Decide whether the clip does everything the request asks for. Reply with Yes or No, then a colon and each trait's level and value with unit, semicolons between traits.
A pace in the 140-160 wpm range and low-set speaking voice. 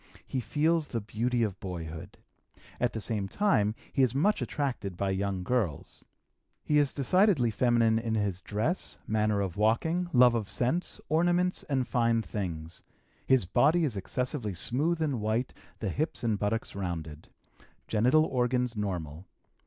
Yes: average, 150 wpm; low, 115 Hz